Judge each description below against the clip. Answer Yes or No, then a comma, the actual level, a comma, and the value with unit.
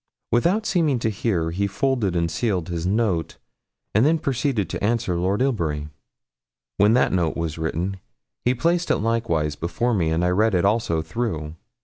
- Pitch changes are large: Yes, wide, 6.1 semitones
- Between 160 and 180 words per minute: Yes, average, 170 wpm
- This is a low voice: Yes, low, 100 Hz